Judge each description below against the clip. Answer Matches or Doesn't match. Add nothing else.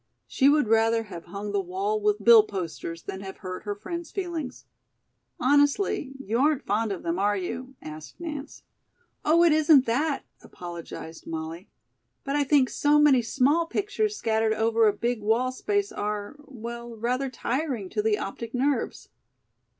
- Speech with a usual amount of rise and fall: Doesn't match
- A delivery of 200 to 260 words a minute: Doesn't match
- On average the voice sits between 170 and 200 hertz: Doesn't match